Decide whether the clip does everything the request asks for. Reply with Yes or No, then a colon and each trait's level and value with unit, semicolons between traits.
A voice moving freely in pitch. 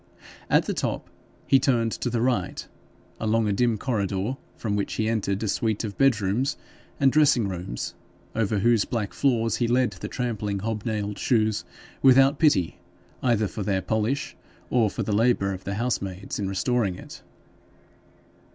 No: average, 3.5 semitones